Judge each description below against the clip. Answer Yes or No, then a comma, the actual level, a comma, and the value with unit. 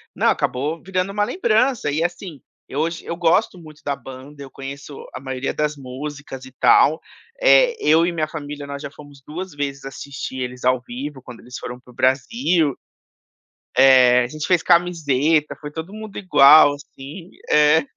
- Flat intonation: No, average, 3.9 semitones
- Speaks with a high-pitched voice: No, medium, 150 Hz